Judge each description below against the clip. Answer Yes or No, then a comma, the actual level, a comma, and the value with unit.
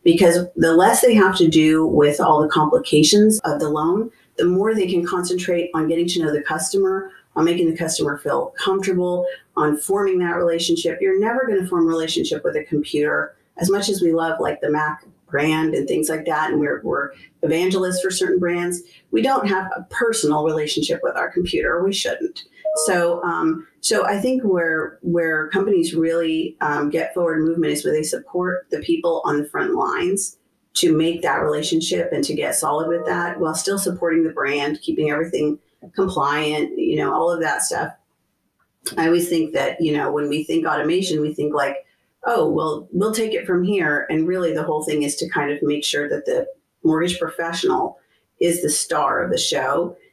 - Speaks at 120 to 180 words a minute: No, average, 195 wpm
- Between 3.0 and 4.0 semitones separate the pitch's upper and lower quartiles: Yes, average, 3.6 semitones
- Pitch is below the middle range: No, medium, 170 Hz